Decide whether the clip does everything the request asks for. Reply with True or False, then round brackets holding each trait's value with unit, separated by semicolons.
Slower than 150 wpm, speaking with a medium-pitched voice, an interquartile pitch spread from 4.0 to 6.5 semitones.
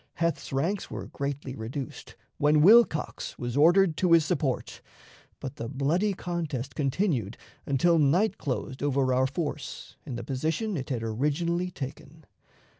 True (140 wpm; 145 Hz; 4.5 semitones)